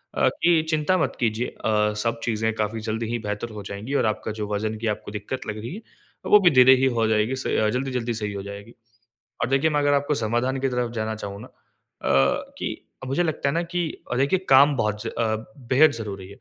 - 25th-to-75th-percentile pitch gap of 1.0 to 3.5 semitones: No, average, 4.2 semitones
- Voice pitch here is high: No, low, 115 Hz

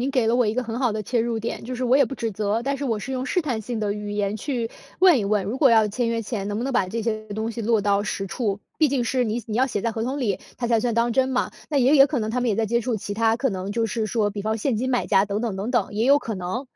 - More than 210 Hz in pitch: Yes, high, 230 Hz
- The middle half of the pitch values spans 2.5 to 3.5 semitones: Yes, average, 3.1 semitones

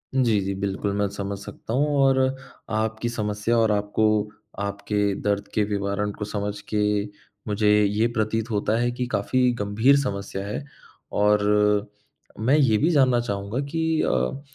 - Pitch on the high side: No, low, 105 Hz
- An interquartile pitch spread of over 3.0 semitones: No, average, 2.7 semitones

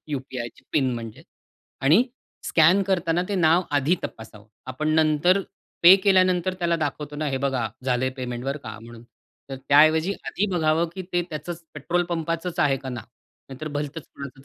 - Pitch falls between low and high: Yes, medium, 155 Hz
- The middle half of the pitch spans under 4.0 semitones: No, average, 4.5 semitones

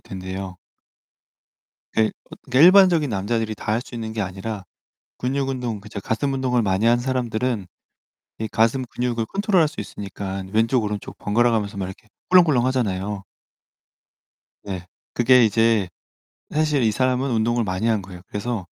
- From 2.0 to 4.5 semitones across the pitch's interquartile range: Yes, average, 3.9 semitones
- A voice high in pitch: No, low, 115 Hz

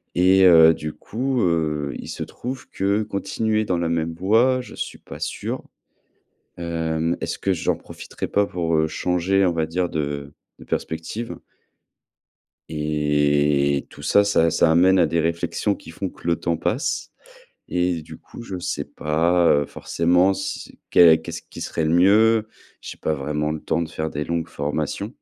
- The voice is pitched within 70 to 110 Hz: Yes, very low, 85 Hz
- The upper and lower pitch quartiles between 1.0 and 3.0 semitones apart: No, average, 3.5 semitones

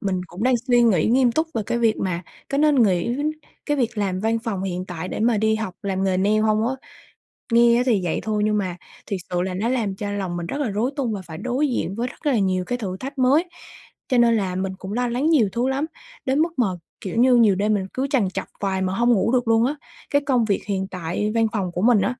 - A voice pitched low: No, high, 220 Hz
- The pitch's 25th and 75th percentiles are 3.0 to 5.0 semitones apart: Yes, average, 4.4 semitones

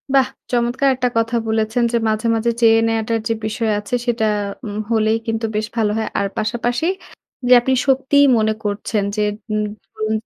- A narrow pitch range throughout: Yes, narrow, 1.8 semitones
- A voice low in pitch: No, high, 225 Hz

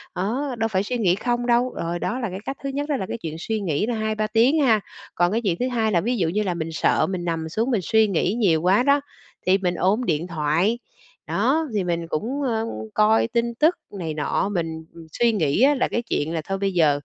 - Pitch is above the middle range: Yes, high, 210 Hz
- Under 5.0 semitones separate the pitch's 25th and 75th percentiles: No, wide, 5.6 semitones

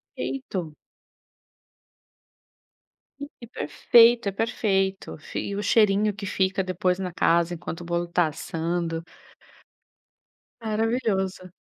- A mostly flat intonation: No, average, 3.7 semitones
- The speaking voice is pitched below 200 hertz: Yes, high, 190 Hz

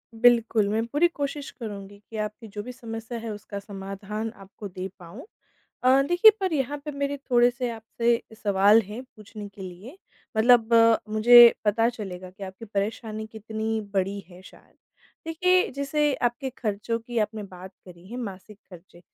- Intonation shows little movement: No, average, 3.4 semitones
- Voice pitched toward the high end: Yes, high, 220 Hz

